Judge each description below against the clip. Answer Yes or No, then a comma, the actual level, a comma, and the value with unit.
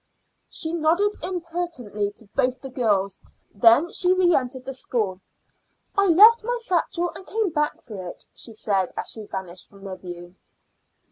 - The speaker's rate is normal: Yes, average, 155 wpm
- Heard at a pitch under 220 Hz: No, very high, 260 Hz